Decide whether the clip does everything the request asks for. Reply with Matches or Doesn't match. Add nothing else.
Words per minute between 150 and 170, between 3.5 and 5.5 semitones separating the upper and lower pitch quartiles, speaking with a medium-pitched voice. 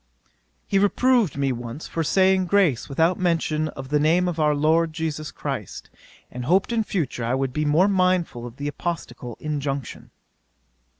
Matches